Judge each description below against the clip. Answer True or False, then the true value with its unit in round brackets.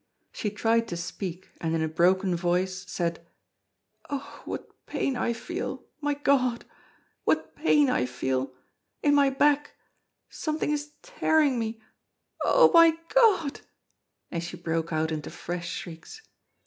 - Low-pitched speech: False (225 Hz)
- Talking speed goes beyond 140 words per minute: False (135 wpm)